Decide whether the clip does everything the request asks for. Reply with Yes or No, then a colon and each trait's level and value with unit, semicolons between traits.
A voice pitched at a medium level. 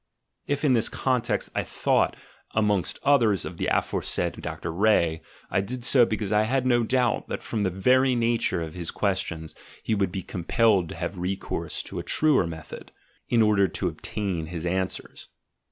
No: low, 105 Hz